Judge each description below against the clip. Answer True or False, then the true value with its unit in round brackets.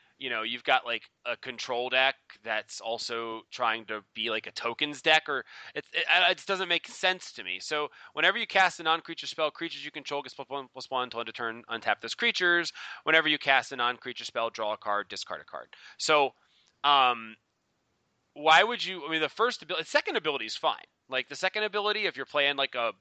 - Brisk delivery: True (225 wpm)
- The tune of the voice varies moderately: False (6.9 semitones)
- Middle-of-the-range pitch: True (145 Hz)